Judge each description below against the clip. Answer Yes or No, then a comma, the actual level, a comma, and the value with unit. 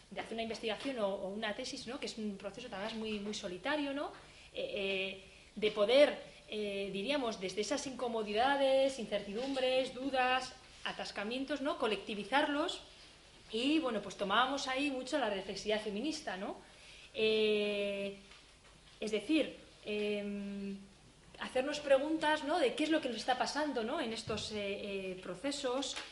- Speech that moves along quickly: No, average, 140 wpm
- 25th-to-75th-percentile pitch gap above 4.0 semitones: Yes, average, 5.0 semitones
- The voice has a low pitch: No, high, 225 Hz